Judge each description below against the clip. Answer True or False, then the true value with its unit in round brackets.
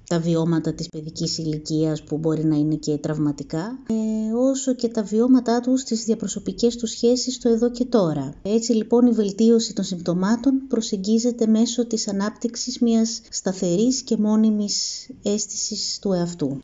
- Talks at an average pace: True (150 wpm)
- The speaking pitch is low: False (220 Hz)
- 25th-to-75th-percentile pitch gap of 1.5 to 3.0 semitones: False (5.6 semitones)